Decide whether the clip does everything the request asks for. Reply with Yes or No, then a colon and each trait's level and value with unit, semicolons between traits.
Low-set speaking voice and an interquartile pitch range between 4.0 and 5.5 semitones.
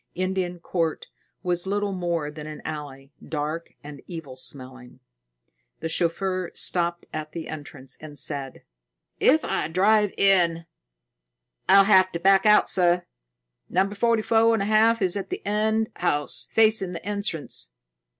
No: medium, 175 Hz; average, 4.5 semitones